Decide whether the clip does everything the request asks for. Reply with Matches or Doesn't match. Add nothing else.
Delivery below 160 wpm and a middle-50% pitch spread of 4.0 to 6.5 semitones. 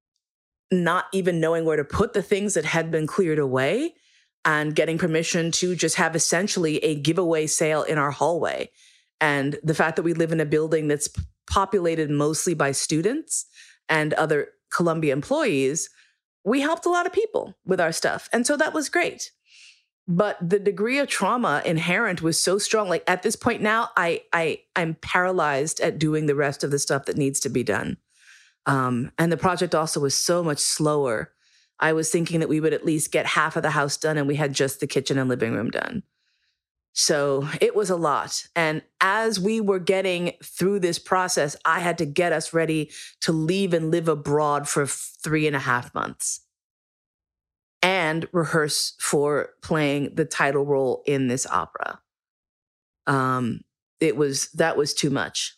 Doesn't match